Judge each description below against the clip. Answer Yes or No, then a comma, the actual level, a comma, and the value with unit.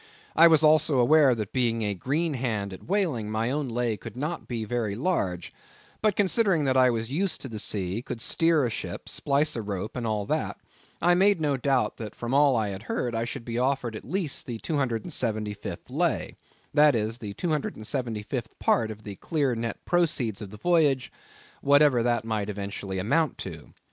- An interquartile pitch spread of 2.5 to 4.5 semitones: No, wide, 5.5 semitones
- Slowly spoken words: No, average, 190 wpm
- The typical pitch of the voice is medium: No, low, 120 Hz